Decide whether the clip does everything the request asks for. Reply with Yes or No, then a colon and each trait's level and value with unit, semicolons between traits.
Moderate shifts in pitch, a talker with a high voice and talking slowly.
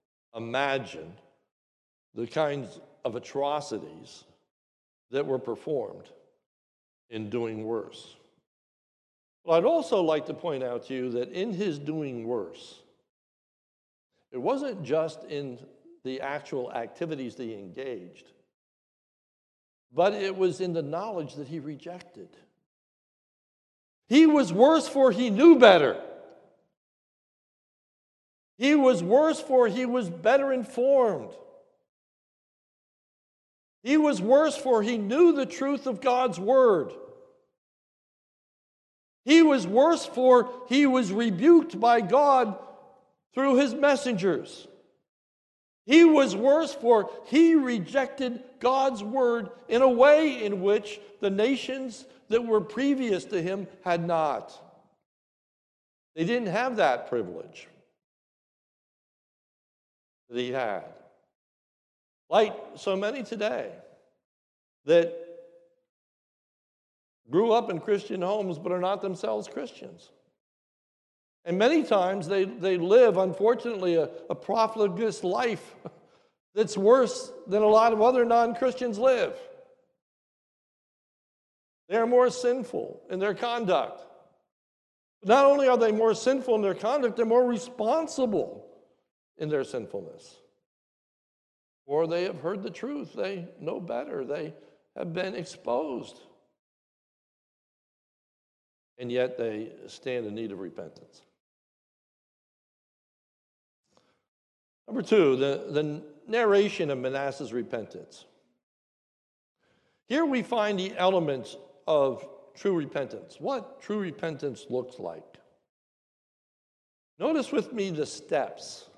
No: wide, 8.1 semitones; high, 215 Hz; slow, 110 wpm